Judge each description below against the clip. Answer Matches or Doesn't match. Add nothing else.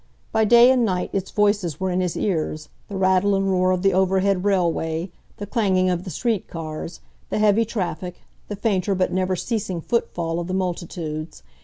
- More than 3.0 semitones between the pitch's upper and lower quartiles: Doesn't match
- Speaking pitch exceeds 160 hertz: Matches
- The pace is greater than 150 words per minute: Matches